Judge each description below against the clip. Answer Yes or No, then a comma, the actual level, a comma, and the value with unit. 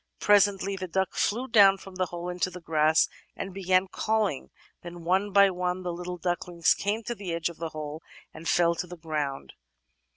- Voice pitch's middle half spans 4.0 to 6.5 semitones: No, narrow, 2.6 semitones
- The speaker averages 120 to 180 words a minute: No, average, 195 wpm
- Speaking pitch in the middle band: Yes, medium, 180 Hz